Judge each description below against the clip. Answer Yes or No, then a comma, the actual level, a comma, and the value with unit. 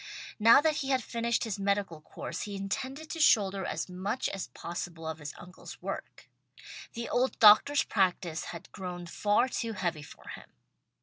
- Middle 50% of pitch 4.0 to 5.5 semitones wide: Yes, average, 4.9 semitones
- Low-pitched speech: No, high, 200 Hz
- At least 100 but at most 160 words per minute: No, average, 170 wpm